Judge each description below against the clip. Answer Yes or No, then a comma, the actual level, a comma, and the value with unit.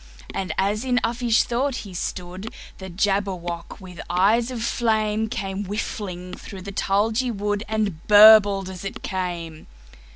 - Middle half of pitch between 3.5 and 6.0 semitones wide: No, average, 2.9 semitones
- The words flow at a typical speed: No, slow, 125 wpm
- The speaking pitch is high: Yes, high, 200 Hz